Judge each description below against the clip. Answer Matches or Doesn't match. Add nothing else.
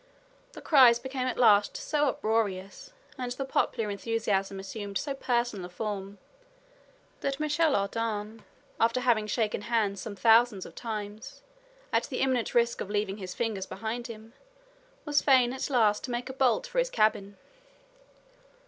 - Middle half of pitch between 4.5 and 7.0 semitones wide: Doesn't match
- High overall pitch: Matches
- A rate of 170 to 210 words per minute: Doesn't match